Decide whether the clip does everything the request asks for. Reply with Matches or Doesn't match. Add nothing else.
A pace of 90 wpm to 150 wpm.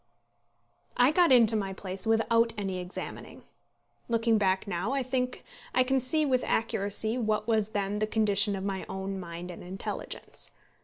Doesn't match